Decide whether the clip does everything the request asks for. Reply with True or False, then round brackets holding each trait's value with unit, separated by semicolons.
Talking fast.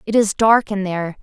True (245 wpm)